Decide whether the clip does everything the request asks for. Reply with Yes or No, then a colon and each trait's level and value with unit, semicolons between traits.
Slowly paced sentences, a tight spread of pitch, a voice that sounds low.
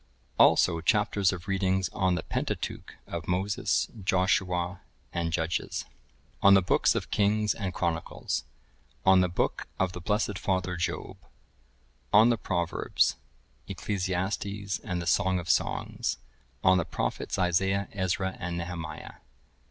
Yes: slow, 130 wpm; narrow, 2.0 semitones; very low, 95 Hz